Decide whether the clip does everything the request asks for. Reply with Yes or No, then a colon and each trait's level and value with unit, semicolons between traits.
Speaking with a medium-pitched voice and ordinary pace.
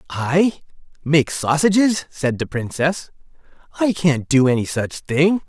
No: medium, 150 Hz; slow, 130 wpm